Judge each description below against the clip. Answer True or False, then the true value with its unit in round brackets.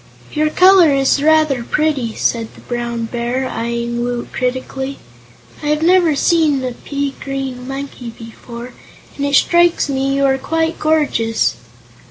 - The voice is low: False (270 Hz)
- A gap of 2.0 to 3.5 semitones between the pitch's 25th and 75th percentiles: False (4.2 semitones)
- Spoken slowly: False (145 wpm)